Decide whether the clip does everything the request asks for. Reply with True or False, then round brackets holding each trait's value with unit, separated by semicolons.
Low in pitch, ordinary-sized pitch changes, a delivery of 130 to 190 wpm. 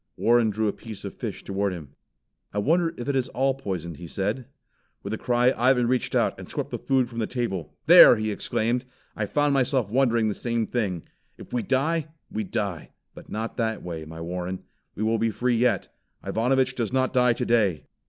False (115 Hz; 3.9 semitones; 200 wpm)